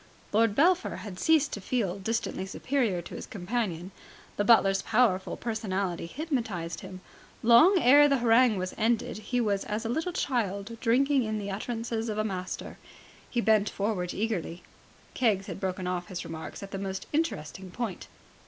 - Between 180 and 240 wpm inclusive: No, average, 165 wpm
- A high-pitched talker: Yes, high, 215 Hz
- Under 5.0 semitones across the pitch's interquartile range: Yes, average, 4.1 semitones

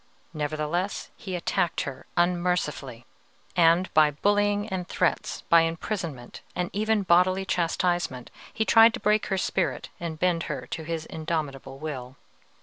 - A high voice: No, medium, 170 Hz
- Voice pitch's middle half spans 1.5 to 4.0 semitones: Yes, average, 3.5 semitones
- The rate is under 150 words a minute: Yes, average, 140 wpm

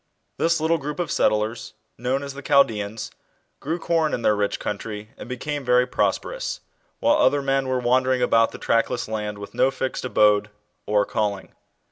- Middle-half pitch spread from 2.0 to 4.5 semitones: No, average, 4.9 semitones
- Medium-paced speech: Yes, average, 175 wpm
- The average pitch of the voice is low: Yes, low, 125 Hz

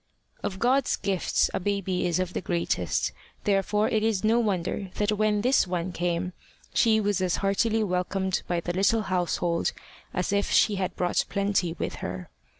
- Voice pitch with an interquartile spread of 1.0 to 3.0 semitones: Yes, average, 2.7 semitones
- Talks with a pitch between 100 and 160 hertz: No, high, 195 Hz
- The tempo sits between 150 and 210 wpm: Yes, average, 170 wpm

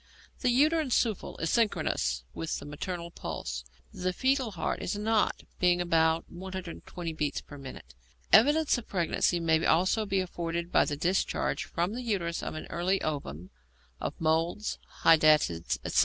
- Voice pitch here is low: No, medium, 175 Hz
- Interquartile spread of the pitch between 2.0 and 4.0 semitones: No, average, 4.5 semitones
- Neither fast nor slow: Yes, average, 155 wpm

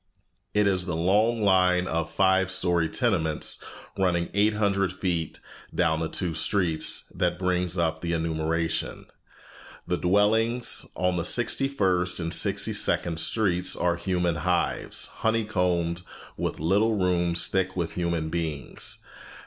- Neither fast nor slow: No, slow, 130 wpm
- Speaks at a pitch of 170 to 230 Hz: No, very low, 90 Hz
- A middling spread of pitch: No, narrow, 2.3 semitones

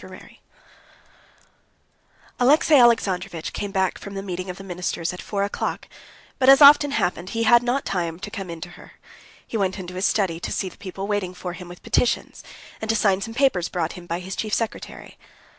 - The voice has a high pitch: Yes, high, 195 Hz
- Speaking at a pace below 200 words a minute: No, fast, 205 wpm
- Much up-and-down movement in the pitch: No, average, 4.0 semitones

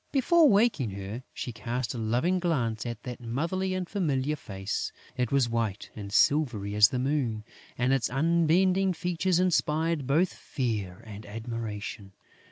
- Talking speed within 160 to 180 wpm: No, average, 150 wpm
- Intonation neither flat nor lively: No, wide, 7.2 semitones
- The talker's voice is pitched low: Yes, low, 130 Hz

